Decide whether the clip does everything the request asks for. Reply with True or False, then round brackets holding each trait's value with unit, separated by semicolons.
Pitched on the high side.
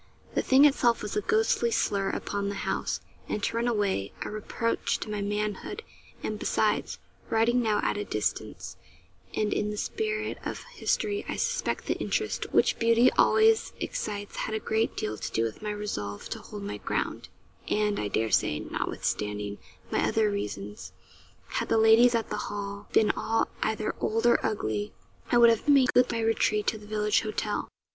True (215 Hz)